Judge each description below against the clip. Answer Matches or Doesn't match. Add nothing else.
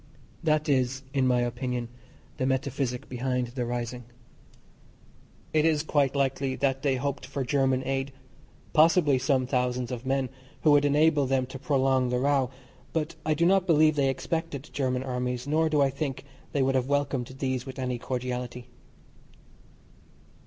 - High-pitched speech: Doesn't match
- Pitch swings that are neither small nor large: Doesn't match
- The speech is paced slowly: Doesn't match